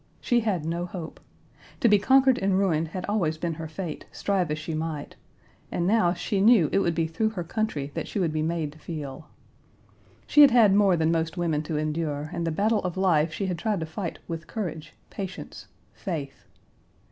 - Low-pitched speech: No, medium, 170 Hz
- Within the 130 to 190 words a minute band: No, fast, 205 wpm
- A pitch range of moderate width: Yes, average, 3.9 semitones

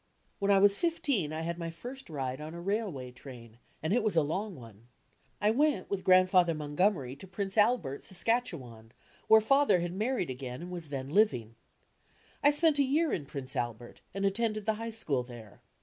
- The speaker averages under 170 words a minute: No, average, 195 wpm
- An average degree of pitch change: No, wide, 8.0 semitones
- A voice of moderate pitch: Yes, medium, 180 Hz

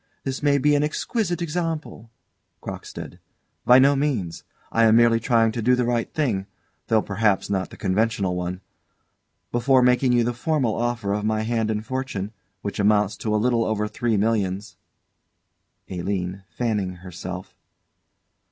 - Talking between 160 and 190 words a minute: No, average, 150 wpm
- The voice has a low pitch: Yes, low, 115 Hz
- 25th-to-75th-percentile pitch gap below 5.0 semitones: Yes, average, 3.8 semitones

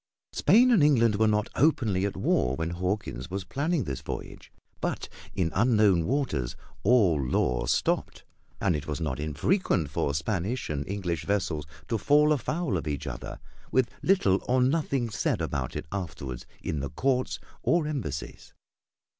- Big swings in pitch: Yes, wide, 8.9 semitones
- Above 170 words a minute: No, average, 155 wpm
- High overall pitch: No, low, 100 Hz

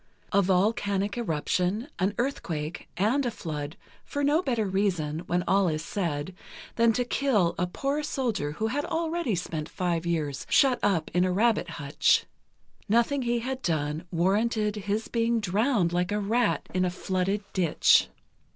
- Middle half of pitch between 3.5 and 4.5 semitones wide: No, average, 5.3 semitones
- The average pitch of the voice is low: No, high, 200 Hz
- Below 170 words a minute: Yes, average, 160 wpm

